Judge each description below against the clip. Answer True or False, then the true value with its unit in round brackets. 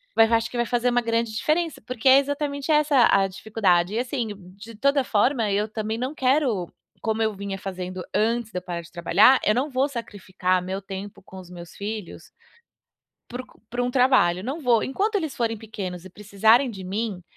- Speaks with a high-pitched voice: True (225 Hz)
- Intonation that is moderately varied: True (4.7 semitones)